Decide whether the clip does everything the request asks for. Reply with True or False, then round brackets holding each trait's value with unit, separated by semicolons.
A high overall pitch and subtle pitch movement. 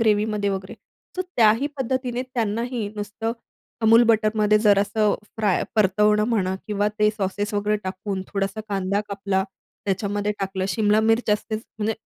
True (210 Hz; 1.7 semitones)